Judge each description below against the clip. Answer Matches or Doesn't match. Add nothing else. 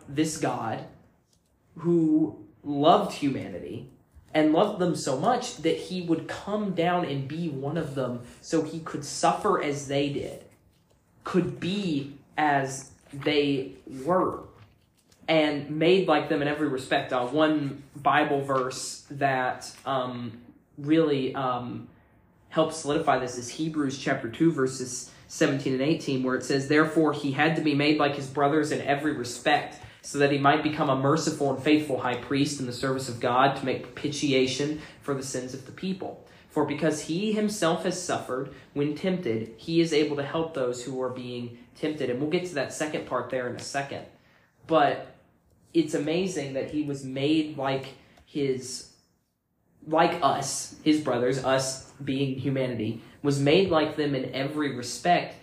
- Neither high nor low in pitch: Matches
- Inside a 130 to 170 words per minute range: Matches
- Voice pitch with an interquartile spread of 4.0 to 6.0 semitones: Doesn't match